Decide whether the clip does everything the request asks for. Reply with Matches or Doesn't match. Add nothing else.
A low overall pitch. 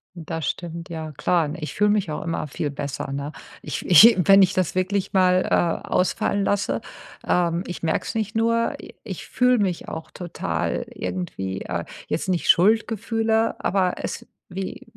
Doesn't match